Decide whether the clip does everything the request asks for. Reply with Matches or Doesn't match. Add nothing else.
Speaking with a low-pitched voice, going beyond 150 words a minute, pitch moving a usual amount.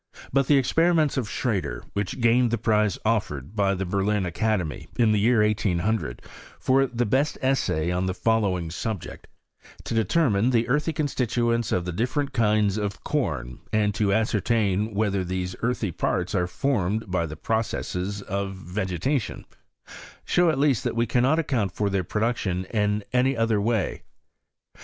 Matches